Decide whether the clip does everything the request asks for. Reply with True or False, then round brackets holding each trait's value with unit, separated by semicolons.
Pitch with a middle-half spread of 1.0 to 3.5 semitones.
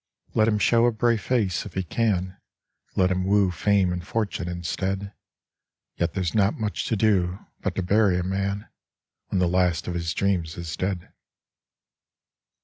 True (2.7 semitones)